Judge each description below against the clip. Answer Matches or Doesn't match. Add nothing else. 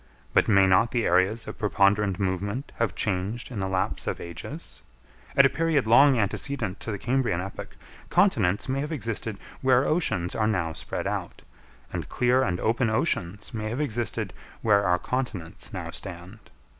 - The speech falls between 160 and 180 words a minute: Matches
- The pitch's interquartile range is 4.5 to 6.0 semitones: Matches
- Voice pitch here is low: Matches